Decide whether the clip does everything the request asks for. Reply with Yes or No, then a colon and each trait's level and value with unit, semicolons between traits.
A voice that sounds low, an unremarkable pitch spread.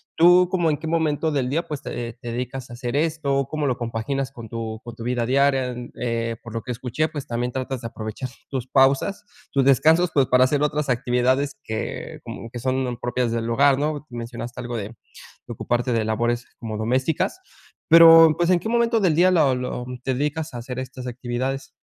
Yes: low, 130 Hz; average, 3.8 semitones